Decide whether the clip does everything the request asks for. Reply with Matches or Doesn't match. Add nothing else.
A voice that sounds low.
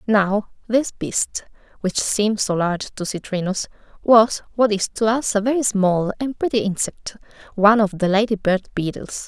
Doesn't match